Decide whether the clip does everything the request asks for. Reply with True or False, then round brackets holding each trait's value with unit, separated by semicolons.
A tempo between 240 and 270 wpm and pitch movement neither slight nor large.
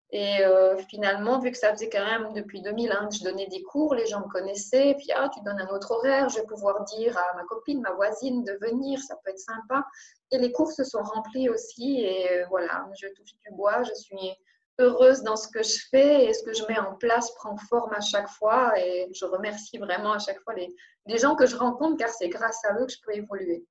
True (255 wpm; 4.2 semitones)